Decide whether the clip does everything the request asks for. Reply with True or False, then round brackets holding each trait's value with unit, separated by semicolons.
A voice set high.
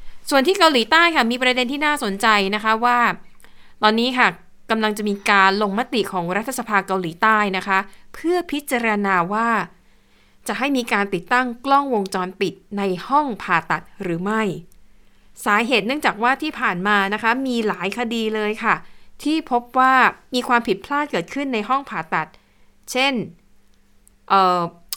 True (215 Hz)